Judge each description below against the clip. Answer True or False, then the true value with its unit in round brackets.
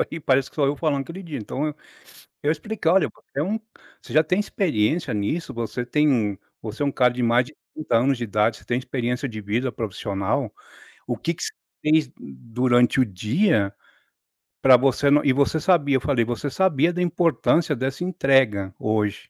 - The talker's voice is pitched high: False (135 Hz)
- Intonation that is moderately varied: True (4.9 semitones)